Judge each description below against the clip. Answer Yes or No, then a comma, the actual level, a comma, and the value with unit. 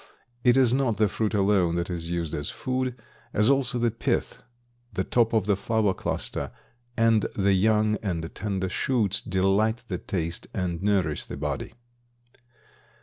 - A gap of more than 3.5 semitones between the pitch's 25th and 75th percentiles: Yes, average, 3.9 semitones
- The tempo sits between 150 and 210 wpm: Yes, average, 155 wpm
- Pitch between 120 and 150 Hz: No, low, 100 Hz